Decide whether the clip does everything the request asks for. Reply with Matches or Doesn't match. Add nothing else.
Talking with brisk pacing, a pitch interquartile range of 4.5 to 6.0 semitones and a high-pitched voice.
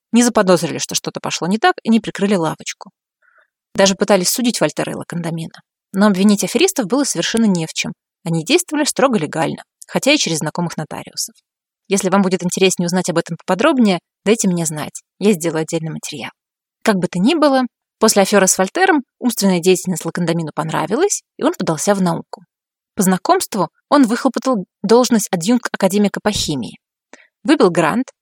Matches